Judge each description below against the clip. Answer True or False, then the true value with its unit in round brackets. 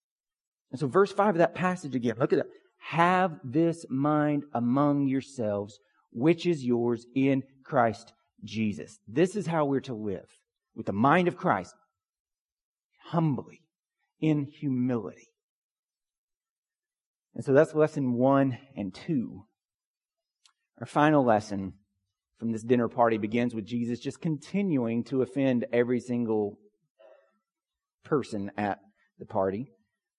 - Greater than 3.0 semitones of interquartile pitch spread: True (5.1 semitones)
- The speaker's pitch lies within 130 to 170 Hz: True (135 Hz)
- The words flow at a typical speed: False (125 wpm)